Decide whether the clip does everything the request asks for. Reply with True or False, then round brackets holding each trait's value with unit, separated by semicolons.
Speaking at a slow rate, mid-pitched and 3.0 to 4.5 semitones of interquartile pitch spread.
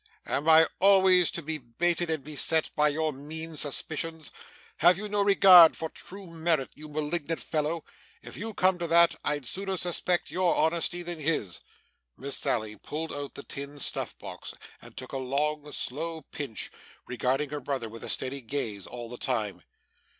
False (170 wpm; 155 Hz; 3.5 semitones)